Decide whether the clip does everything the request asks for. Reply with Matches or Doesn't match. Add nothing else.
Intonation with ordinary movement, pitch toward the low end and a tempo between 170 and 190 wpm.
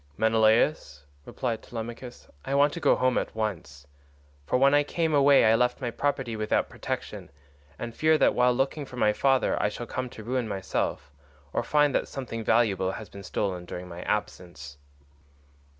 Matches